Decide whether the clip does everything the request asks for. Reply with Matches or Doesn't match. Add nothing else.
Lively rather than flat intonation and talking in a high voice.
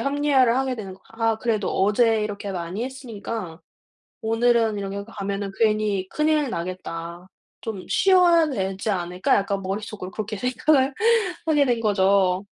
Doesn't match